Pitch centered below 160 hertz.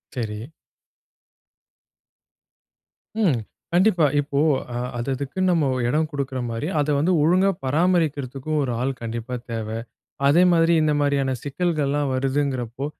Yes: medium, 140 Hz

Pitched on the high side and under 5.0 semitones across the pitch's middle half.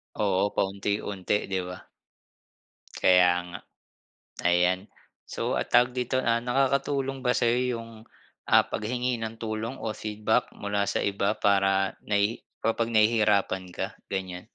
No: low, 105 Hz; average, 3.2 semitones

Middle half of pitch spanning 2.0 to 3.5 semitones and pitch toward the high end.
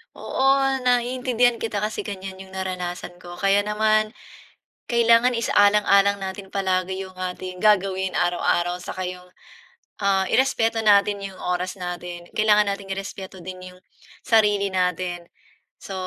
Yes: average, 2.7 semitones; high, 195 Hz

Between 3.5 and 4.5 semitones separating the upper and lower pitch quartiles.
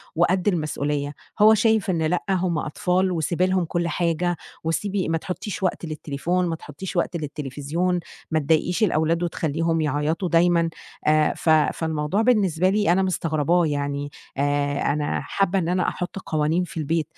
No: average, 3.0 semitones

